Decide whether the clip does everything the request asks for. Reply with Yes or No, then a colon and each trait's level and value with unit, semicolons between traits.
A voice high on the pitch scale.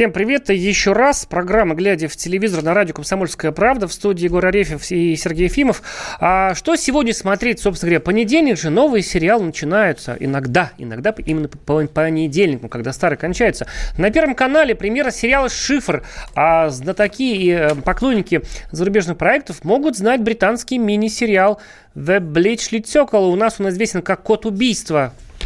Yes: high, 195 Hz